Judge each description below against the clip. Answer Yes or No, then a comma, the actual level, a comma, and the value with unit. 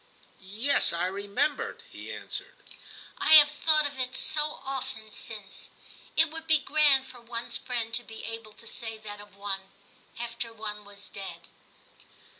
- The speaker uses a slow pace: No, average, 165 wpm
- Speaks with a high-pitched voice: Yes, high, 230 Hz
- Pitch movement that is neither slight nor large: Yes, average, 5.0 semitones